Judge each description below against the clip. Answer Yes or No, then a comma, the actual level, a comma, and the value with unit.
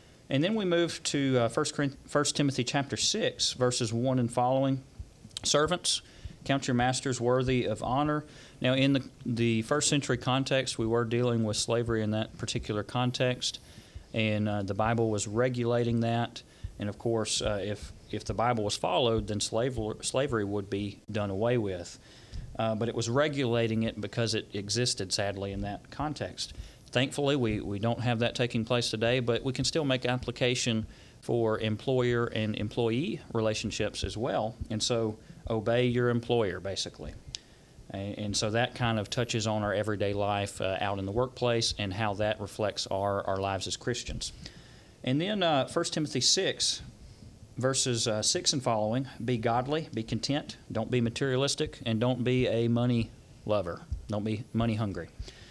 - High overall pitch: No, low, 115 Hz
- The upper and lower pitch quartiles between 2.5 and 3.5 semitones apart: Yes, average, 2.9 semitones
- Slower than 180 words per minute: Yes, average, 170 wpm